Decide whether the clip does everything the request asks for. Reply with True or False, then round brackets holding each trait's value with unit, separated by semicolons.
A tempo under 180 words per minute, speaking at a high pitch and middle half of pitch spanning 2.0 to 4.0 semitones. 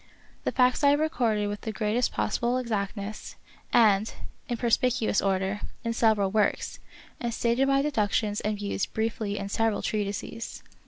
True (155 wpm; 220 Hz; 2.7 semitones)